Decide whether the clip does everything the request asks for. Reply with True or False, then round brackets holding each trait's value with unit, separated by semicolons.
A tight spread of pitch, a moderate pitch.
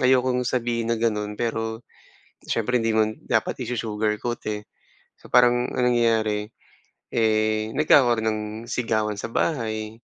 False (2.1 semitones; 115 Hz)